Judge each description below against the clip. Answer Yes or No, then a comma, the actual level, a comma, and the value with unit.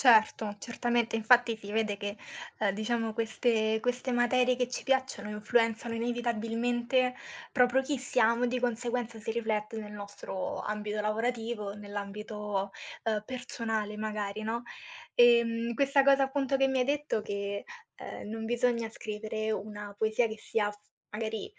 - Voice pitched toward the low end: No, high, 225 Hz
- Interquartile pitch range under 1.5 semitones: No, narrow, 2.5 semitones